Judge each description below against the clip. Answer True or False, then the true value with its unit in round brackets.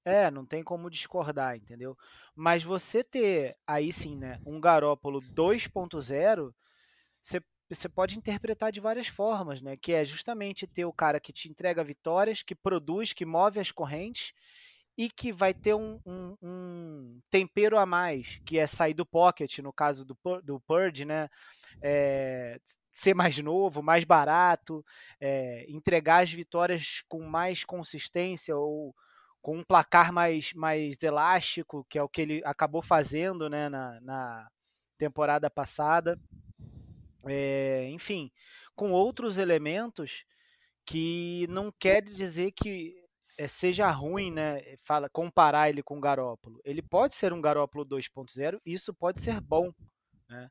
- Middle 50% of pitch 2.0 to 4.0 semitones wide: False (4.5 semitones)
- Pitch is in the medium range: True (165 Hz)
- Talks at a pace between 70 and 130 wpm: False (145 wpm)